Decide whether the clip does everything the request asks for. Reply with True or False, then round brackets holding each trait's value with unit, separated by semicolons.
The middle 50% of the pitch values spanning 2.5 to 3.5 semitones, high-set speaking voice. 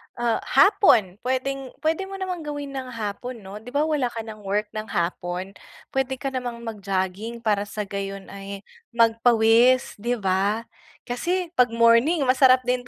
False (4.2 semitones; 235 Hz)